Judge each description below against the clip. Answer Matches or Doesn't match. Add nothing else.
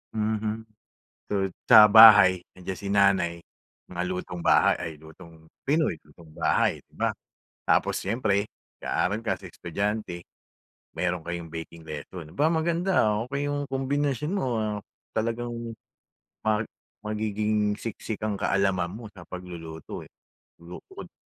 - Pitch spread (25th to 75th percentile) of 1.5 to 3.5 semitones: Doesn't match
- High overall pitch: Doesn't match